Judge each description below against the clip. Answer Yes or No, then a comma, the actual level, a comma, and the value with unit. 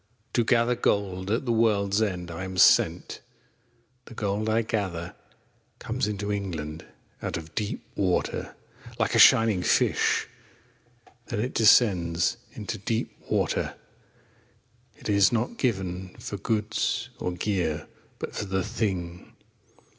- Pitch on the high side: No, low, 100 Hz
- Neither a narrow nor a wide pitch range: Yes, average, 3.4 semitones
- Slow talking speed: Yes, slow, 130 wpm